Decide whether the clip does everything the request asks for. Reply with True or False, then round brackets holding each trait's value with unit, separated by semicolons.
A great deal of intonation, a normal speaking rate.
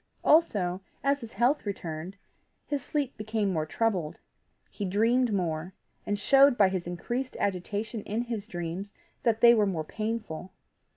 False (4.7 semitones; 150 wpm)